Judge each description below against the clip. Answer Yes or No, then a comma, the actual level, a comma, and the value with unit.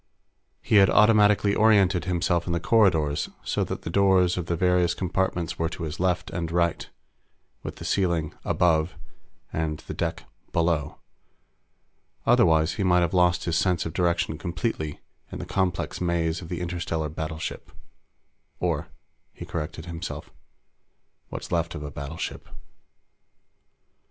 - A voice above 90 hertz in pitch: No, very low, 85 Hz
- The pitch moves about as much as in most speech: No, narrow, 2.1 semitones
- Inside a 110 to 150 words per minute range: Yes, average, 140 wpm